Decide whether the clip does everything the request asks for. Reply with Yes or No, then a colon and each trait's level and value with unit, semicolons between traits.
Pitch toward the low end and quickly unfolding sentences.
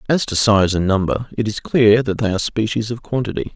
Yes: low, 110 Hz; fast, 235 wpm